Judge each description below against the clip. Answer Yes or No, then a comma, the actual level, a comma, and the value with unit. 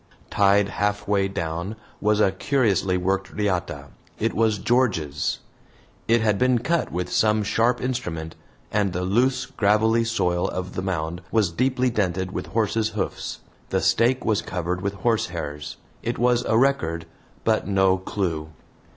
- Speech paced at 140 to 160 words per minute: Yes, average, 145 wpm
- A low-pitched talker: Yes, low, 100 Hz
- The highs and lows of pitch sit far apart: No, average, 4.0 semitones